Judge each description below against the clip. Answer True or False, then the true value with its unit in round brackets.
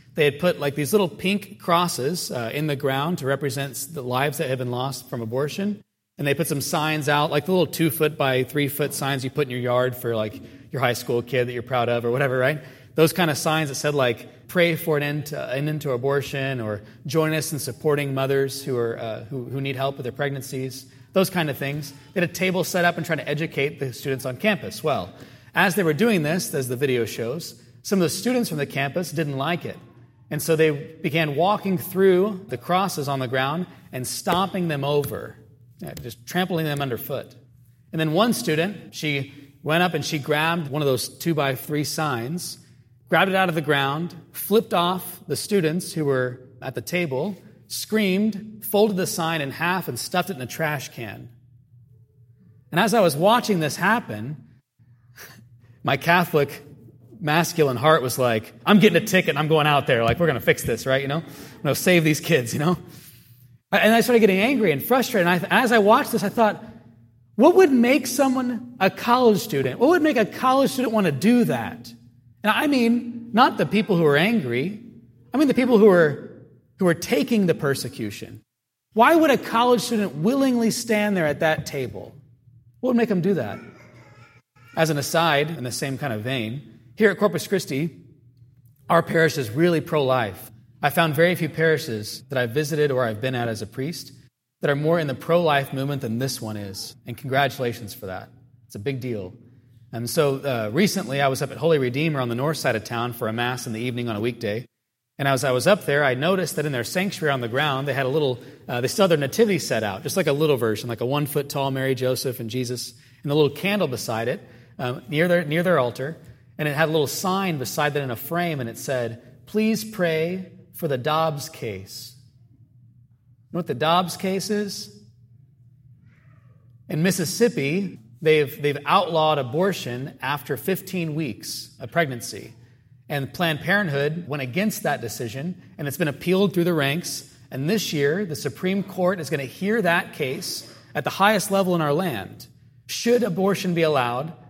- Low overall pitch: False (145 Hz)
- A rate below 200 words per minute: False (205 wpm)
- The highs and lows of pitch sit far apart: True (5.8 semitones)